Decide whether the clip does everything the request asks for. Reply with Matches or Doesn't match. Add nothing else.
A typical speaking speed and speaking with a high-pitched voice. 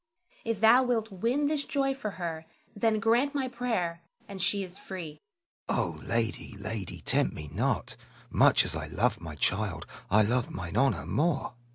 Doesn't match